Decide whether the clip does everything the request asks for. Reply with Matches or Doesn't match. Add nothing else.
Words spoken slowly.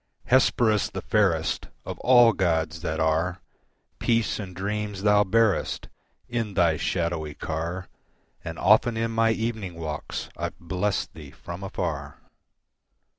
Matches